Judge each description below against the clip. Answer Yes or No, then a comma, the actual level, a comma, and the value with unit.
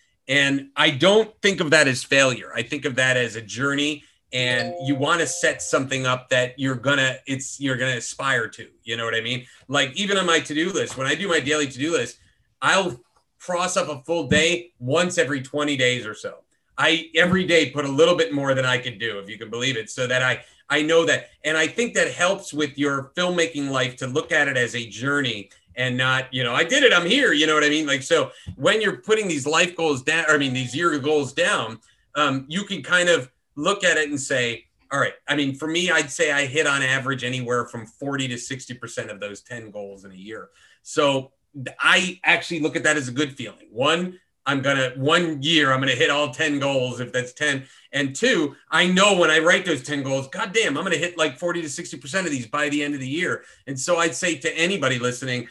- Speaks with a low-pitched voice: No, medium, 145 Hz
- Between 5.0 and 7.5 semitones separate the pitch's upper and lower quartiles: No, average, 4.1 semitones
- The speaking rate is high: Yes, fast, 240 wpm